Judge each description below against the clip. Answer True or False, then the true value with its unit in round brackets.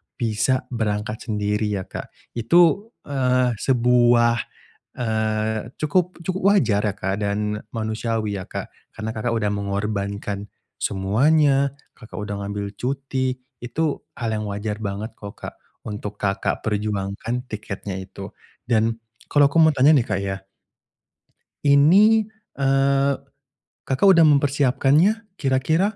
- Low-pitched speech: True (115 Hz)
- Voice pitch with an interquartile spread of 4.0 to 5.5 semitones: True (4.9 semitones)